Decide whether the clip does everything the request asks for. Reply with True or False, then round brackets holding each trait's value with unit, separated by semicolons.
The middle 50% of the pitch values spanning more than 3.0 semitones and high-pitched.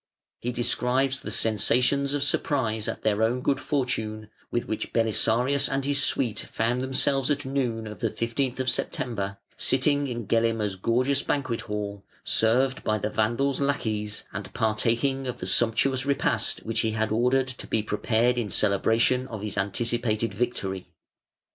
False (3.4 semitones; 120 Hz)